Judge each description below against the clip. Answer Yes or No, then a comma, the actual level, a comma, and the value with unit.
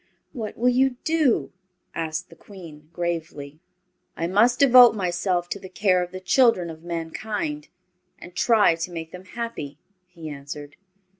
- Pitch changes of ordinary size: No, wide, 5.9 semitones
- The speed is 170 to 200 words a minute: No, average, 150 wpm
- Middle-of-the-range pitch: Yes, medium, 180 Hz